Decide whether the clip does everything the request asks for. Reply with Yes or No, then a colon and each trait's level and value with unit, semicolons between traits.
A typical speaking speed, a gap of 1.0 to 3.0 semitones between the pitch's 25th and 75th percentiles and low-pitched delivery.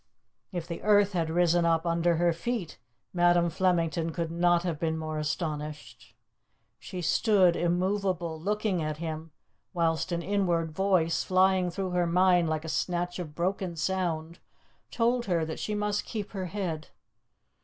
No: average, 155 wpm; narrow, 2.5 semitones; medium, 175 Hz